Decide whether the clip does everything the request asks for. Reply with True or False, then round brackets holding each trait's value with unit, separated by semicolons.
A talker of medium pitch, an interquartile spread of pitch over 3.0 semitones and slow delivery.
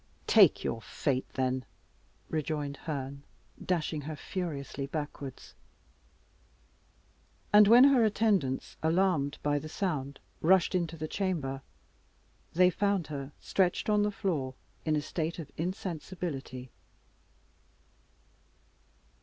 True (155 Hz; 4.8 semitones; 105 wpm)